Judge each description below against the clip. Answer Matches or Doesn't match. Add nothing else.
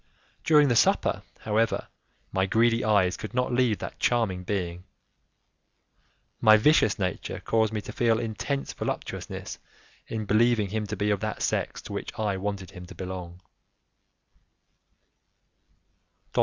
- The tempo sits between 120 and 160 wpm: Matches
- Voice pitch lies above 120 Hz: Doesn't match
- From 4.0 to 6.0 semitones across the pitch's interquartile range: Doesn't match